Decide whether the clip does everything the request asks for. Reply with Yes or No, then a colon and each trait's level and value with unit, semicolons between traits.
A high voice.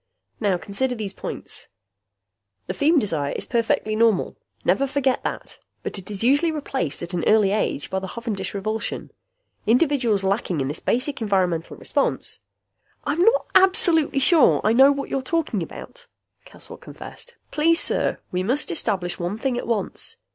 Yes: high, 230 Hz